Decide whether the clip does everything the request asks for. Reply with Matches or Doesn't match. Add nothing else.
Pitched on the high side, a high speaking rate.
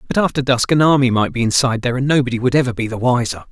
Doesn't match